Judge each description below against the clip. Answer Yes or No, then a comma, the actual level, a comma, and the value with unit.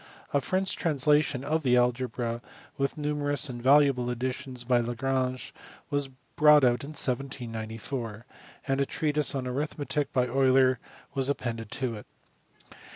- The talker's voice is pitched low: Yes, low, 130 Hz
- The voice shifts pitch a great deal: No, average, 2.7 semitones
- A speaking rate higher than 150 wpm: No, slow, 135 wpm